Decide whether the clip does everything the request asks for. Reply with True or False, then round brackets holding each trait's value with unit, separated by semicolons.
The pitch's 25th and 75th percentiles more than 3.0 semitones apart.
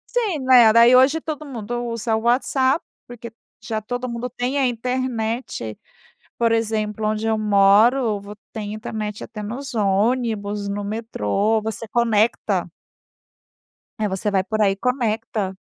False (2.7 semitones)